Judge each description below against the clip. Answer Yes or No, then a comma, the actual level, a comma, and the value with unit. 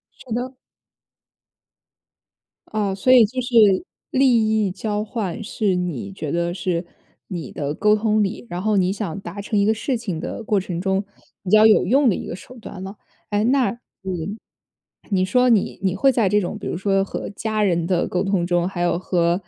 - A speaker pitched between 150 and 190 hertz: No, high, 200 Hz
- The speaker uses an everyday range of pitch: Yes, average, 3.5 semitones